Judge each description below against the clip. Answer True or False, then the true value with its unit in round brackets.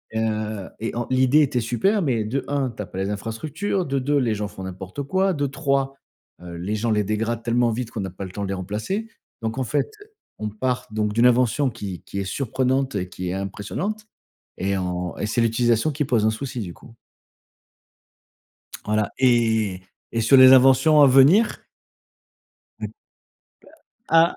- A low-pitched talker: True (115 Hz)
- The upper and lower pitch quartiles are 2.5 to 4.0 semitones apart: False (4.5 semitones)